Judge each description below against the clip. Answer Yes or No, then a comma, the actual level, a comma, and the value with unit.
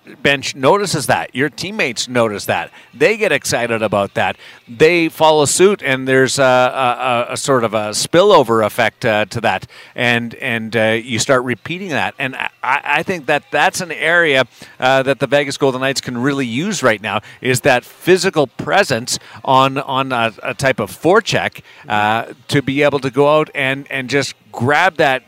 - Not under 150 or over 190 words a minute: Yes, average, 185 wpm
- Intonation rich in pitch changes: No, average, 3.6 semitones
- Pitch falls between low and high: No, low, 130 Hz